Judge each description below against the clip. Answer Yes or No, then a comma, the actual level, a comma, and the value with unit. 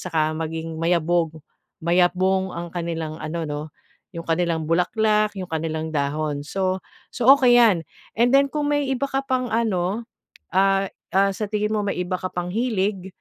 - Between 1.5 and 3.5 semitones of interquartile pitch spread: No, average, 4.5 semitones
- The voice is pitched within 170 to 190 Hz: Yes, medium, 185 Hz